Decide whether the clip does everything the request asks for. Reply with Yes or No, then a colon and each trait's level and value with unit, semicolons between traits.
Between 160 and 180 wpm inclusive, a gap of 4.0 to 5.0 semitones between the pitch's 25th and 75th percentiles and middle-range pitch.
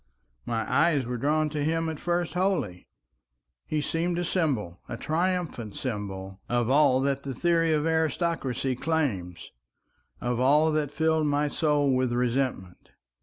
No: average, 145 wpm; average, 4.6 semitones; medium, 145 Hz